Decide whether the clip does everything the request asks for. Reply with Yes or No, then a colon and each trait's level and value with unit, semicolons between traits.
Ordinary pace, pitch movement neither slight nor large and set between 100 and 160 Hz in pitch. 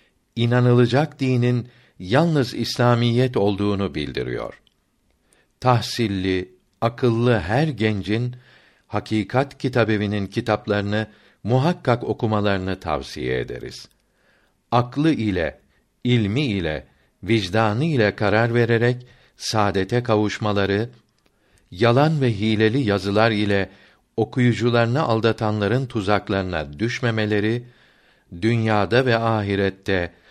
No: slow, 75 wpm; average, 3.3 semitones; low, 110 Hz